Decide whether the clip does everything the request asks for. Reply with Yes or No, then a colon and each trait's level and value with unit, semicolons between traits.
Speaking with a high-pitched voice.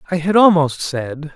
No: medium, 160 Hz